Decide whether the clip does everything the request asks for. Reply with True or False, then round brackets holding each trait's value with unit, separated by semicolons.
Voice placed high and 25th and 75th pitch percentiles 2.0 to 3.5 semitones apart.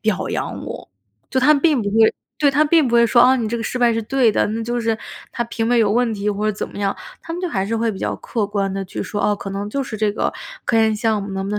True (225 Hz; 2.9 semitones)